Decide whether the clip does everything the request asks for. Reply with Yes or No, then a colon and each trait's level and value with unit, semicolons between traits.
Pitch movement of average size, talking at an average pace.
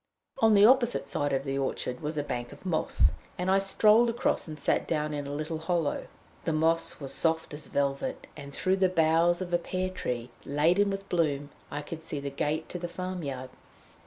No: average, 4.3 semitones; fast, 210 wpm